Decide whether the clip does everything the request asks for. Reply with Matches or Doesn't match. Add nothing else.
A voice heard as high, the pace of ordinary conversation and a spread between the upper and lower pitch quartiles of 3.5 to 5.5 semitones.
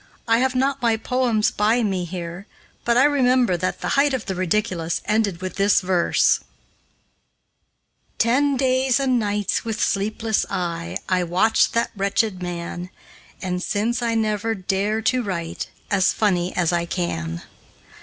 Matches